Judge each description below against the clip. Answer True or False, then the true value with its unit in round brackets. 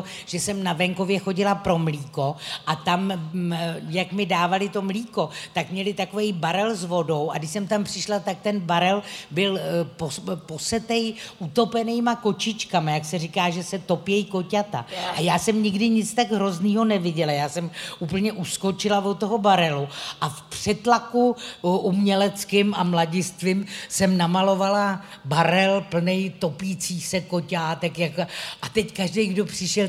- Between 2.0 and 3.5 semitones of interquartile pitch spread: True (2.8 semitones)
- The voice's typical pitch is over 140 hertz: True (190 Hz)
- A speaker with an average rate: True (145 wpm)